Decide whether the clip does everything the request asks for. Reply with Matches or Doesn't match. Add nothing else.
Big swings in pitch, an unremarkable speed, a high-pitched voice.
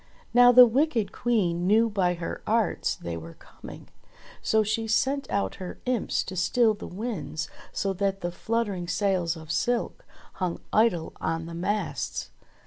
Doesn't match